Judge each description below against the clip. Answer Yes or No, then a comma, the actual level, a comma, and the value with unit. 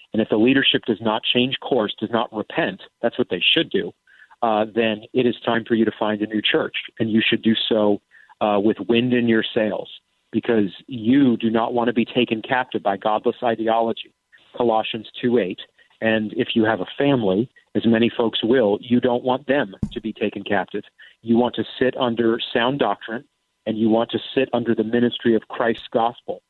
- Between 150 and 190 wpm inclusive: No, fast, 205 wpm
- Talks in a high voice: No, low, 115 Hz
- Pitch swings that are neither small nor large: No, narrow, 1.6 semitones